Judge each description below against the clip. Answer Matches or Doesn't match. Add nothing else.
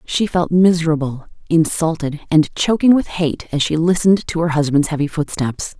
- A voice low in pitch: Doesn't match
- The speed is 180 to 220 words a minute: Doesn't match